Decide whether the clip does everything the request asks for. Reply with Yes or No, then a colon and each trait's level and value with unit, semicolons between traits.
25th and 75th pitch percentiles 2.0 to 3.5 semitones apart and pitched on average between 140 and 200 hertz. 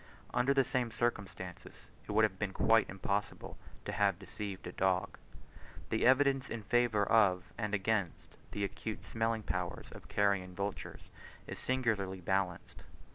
No: average, 3.0 semitones; low, 100 Hz